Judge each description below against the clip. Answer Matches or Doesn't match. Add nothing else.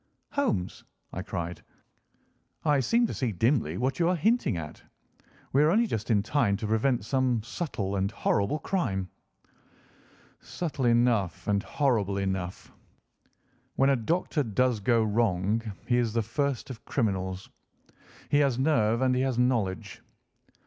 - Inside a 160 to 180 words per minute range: Doesn't match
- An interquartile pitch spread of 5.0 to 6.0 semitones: Matches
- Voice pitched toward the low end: Matches